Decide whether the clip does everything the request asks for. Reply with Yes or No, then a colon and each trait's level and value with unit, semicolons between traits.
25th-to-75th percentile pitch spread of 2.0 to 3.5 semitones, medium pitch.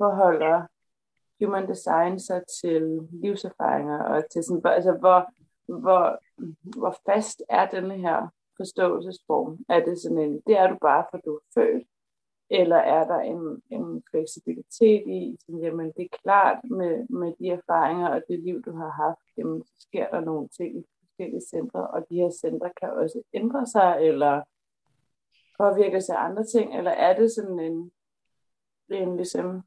Yes: average, 2.8 semitones; medium, 175 Hz